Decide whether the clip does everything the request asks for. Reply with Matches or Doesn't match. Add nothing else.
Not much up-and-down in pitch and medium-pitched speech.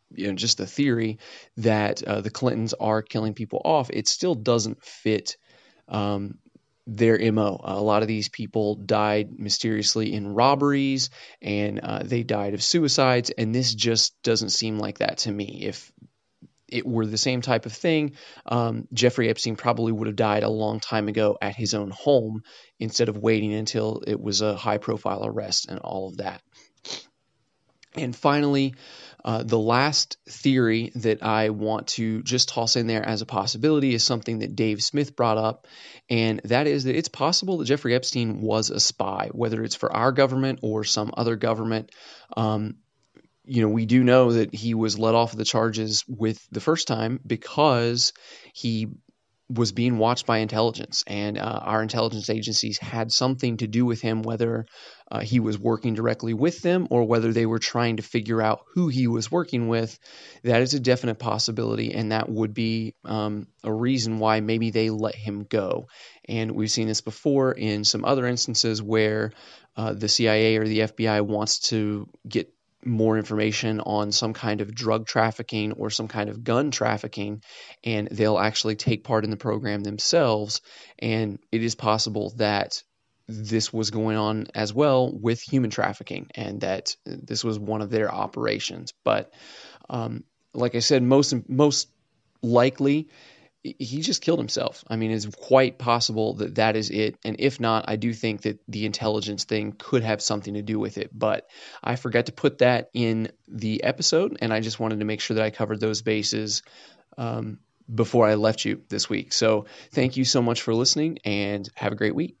Doesn't match